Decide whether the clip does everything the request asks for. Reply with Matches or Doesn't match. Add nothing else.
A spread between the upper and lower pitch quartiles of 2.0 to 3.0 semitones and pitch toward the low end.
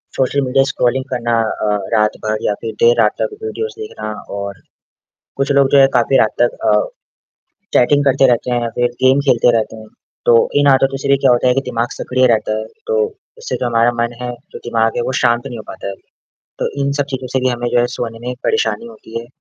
Matches